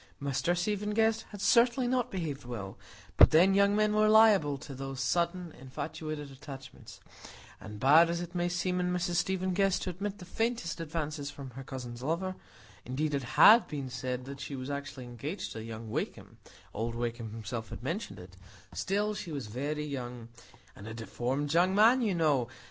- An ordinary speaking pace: Yes, average, 175 wpm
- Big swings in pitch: Yes, wide, 6.5 semitones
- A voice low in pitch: No, medium, 150 Hz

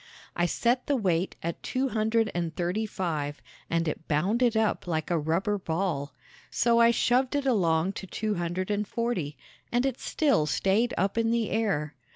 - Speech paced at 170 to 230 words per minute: Yes, average, 180 wpm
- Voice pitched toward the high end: Yes, high, 195 Hz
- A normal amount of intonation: No, wide, 5.7 semitones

